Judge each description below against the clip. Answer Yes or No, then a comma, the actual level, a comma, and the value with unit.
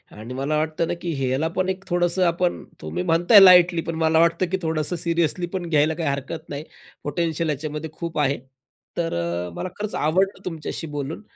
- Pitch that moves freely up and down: No, average, 2.9 semitones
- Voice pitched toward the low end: No, medium, 165 Hz